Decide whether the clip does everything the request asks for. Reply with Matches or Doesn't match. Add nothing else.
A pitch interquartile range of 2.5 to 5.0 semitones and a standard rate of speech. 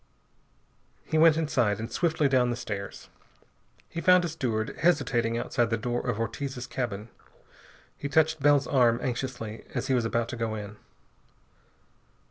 Matches